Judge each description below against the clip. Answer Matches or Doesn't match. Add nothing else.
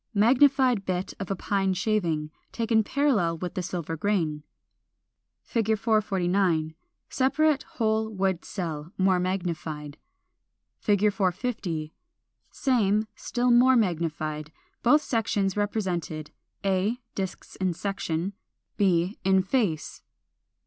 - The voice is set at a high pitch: Matches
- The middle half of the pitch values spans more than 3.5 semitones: Matches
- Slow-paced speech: Matches